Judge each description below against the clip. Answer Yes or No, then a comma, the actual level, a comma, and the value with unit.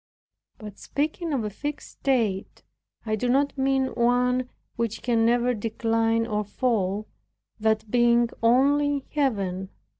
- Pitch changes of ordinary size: Yes, average, 3.4 semitones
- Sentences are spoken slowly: Yes, slow, 130 wpm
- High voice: Yes, high, 235 Hz